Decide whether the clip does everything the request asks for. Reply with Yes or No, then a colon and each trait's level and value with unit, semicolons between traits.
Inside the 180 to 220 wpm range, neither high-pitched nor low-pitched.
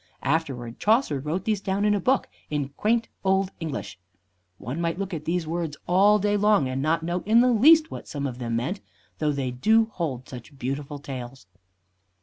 Yes: average, 195 wpm; medium, 165 Hz